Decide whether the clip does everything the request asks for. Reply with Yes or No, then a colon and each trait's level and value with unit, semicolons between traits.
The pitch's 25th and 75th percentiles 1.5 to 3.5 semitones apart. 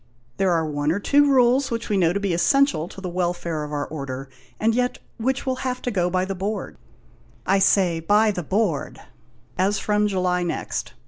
No: average, 4.6 semitones